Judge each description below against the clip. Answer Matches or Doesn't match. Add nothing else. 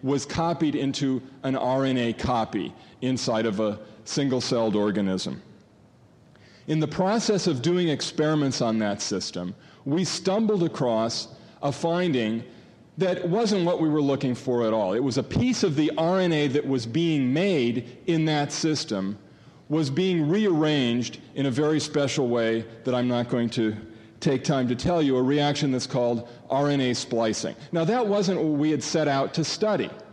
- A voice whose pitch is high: Doesn't match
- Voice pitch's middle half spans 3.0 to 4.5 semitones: Doesn't match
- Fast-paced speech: Doesn't match